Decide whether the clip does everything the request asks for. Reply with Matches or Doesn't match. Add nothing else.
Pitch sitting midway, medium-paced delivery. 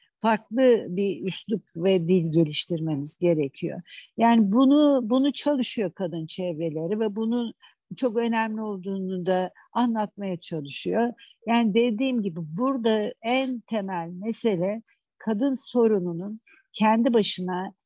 Doesn't match